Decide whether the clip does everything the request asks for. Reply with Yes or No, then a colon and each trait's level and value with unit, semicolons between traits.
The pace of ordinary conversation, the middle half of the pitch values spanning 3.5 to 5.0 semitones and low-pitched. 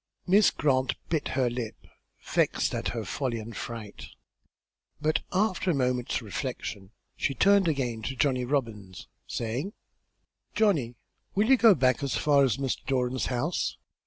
Yes: average, 145 wpm; average, 4.6 semitones; low, 130 Hz